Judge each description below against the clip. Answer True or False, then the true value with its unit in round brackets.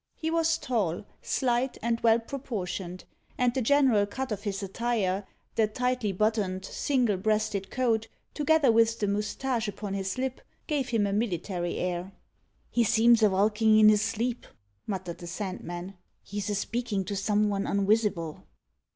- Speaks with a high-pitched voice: True (215 Hz)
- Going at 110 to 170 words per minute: True (155 wpm)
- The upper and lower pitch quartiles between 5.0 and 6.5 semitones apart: False (3.4 semitones)